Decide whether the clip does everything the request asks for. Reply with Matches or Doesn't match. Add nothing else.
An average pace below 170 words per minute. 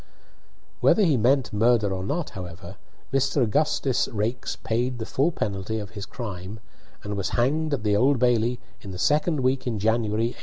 Doesn't match